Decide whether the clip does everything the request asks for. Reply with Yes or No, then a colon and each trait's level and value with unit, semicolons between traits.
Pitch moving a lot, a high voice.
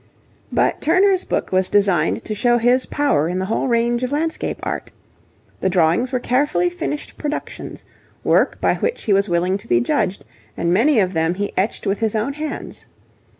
Yes: wide, 7.1 semitones; high, 220 Hz